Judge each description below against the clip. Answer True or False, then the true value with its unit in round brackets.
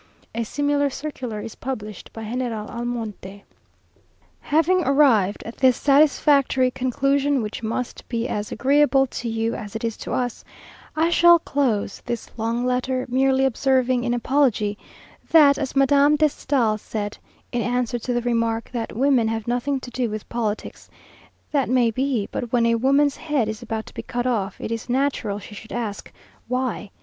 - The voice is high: True (245 Hz)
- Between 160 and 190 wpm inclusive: True (170 wpm)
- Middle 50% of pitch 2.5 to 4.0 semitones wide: True (3.5 semitones)